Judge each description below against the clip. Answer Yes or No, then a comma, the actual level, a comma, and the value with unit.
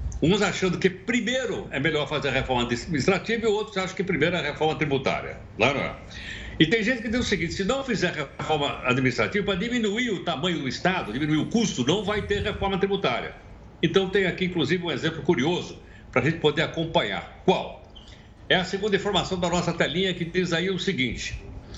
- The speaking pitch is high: No, medium, 180 Hz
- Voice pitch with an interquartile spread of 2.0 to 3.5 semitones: No, average, 4.4 semitones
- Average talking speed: No, fast, 200 wpm